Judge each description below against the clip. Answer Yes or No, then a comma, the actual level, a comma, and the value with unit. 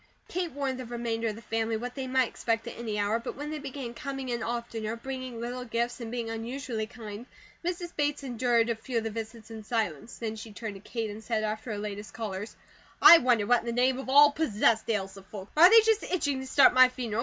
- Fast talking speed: Yes, fast, 240 wpm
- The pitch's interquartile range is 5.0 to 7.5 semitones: No, average, 2.9 semitones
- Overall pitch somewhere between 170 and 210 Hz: No, high, 235 Hz